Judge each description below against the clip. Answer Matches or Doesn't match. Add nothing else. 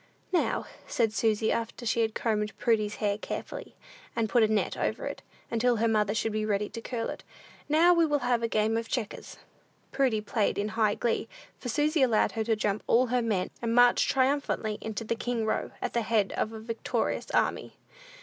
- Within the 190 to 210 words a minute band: Matches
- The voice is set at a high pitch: Matches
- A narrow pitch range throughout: Matches